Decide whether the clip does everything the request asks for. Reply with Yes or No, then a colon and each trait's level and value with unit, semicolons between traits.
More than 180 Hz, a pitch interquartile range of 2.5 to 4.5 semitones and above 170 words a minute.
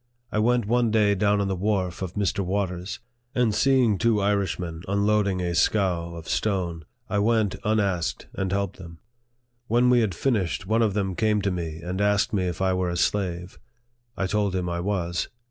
No: low, 100 Hz; average, 3.0 semitones; average, 190 wpm